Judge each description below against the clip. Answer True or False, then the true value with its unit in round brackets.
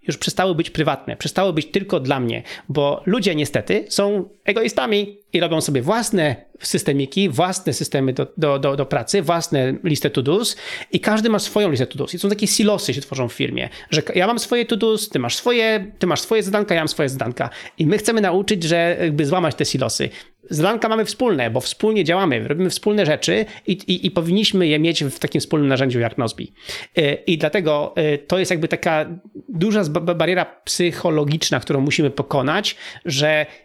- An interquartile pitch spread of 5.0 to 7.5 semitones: True (5.3 semitones)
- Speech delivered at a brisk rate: True (185 wpm)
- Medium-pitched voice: True (170 Hz)